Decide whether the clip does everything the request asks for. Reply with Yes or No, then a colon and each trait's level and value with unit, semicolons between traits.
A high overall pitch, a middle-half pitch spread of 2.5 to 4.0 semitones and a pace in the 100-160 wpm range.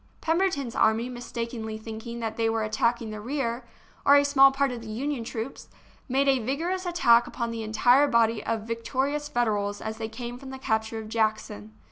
No: high, 235 Hz; average, 3.6 semitones; average, 185 wpm